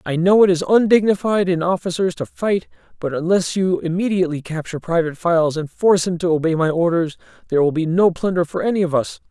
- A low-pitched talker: No, medium, 170 Hz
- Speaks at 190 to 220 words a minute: Yes, fast, 205 wpm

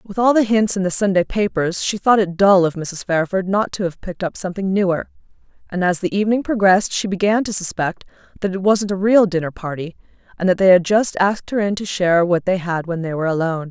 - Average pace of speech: No, fast, 240 wpm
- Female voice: Yes, female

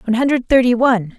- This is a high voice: Yes, high, 240 Hz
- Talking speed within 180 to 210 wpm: Yes, fast, 205 wpm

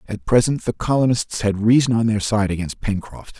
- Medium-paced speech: Yes, average, 195 wpm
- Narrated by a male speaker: Yes, male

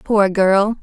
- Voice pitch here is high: Yes, high, 200 Hz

